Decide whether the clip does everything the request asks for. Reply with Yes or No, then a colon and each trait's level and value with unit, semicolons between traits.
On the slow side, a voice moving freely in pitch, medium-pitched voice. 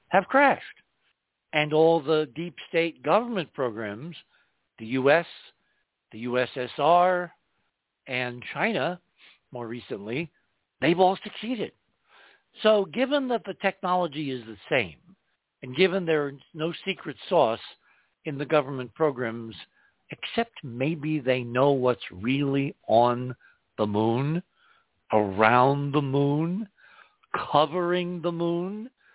Yes: slow, 110 wpm; wide, 6.1 semitones; medium, 155 Hz